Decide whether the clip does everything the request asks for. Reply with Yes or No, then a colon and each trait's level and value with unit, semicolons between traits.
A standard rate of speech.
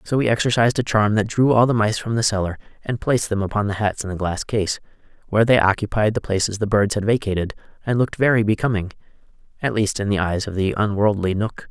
No: fast, 225 wpm